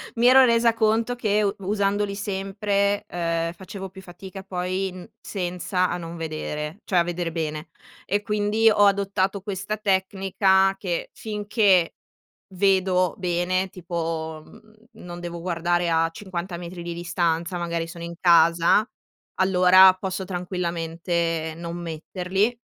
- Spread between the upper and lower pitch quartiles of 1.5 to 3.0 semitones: Yes, average, 2.7 semitones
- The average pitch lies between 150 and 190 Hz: Yes, medium, 185 Hz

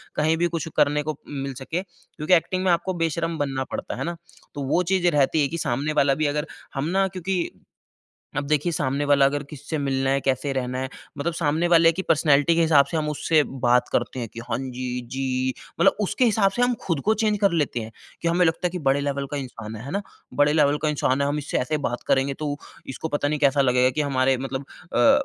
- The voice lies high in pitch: No, medium, 145 Hz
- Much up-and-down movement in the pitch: No, average, 3.7 semitones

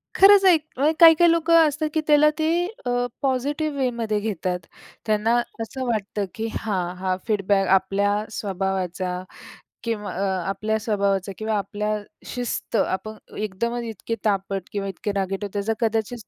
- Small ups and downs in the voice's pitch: No, average, 4.0 semitones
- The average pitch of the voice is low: No, high, 215 Hz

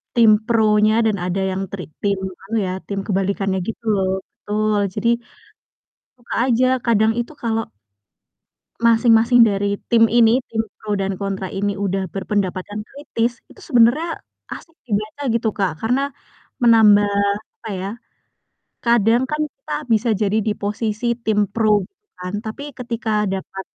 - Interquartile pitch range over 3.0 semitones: No, average, 2.7 semitones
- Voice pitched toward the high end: Yes, high, 215 Hz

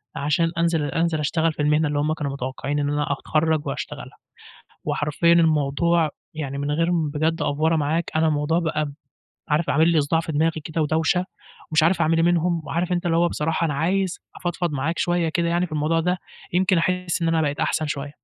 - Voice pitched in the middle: Yes, medium, 160 Hz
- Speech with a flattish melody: Yes, narrow, 2.2 semitones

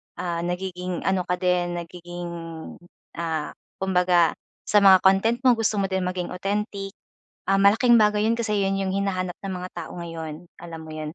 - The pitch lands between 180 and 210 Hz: Yes, medium, 185 Hz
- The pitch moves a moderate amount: No, narrow, 2.2 semitones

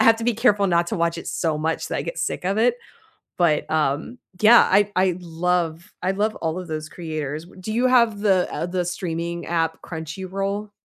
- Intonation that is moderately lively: Yes, average, 4.0 semitones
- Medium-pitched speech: Yes, medium, 180 Hz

